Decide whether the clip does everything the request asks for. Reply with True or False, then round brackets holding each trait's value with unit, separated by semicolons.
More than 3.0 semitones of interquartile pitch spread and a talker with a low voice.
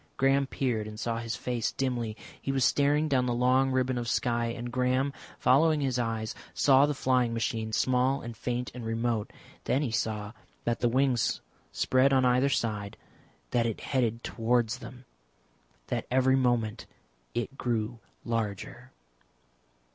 False (2.4 semitones; 125 Hz)